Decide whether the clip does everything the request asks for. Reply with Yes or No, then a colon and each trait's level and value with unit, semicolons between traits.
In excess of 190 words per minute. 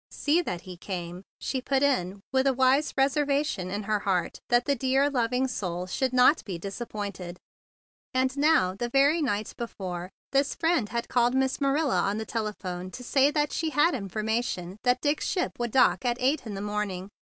Yes: average, 200 wpm